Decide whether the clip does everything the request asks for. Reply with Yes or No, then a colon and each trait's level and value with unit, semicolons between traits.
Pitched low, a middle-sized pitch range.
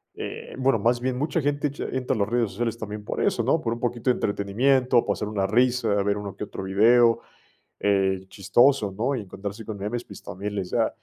Yes: low, 115 Hz; average, 3.7 semitones